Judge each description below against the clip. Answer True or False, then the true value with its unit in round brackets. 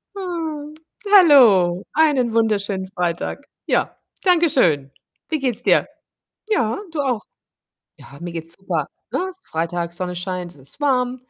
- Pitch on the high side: True (220 Hz)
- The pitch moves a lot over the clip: True (8.8 semitones)